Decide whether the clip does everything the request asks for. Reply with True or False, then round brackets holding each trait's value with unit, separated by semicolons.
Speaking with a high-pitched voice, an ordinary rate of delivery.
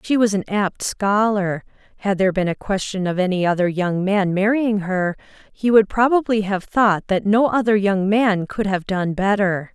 True (200 Hz; 190 wpm)